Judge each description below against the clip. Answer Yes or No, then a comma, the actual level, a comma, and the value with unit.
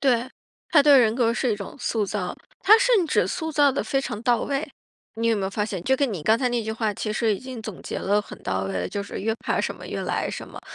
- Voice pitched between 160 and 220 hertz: No, high, 230 Hz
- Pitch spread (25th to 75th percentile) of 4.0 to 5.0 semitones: Yes, average, 4.5 semitones